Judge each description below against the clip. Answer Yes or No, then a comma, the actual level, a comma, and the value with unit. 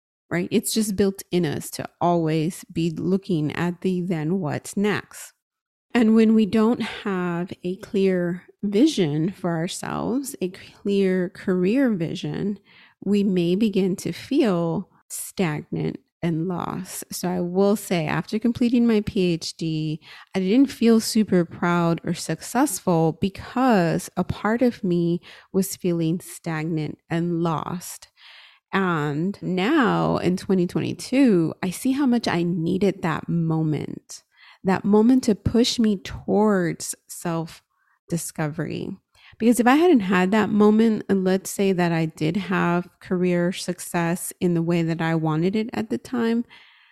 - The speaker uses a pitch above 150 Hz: Yes, medium, 185 Hz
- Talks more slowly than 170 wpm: Yes, average, 140 wpm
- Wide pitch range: No, average, 3.7 semitones